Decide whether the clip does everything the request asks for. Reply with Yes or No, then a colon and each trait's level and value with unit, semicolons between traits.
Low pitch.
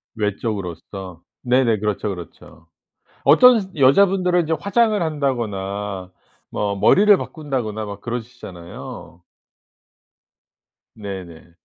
Yes: low, 110 Hz